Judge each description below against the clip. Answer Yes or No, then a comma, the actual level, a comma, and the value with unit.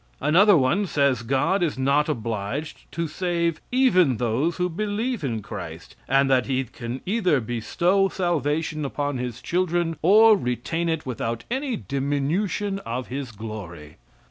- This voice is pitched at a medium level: Yes, medium, 150 Hz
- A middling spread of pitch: No, wide, 6.2 semitones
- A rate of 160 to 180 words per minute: No, average, 145 wpm